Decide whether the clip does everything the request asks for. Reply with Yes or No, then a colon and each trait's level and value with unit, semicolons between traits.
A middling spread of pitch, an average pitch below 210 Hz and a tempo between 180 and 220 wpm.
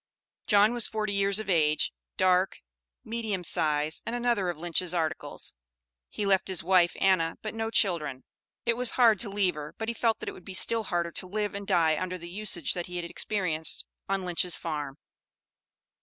Yes: average, 3.8 semitones; medium, 185 Hz; average, 190 wpm